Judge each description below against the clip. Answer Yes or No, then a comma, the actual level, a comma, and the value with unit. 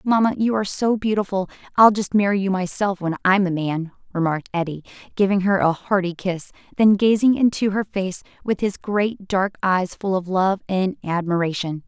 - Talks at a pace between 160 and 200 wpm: Yes, average, 180 wpm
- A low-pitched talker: No, high, 195 Hz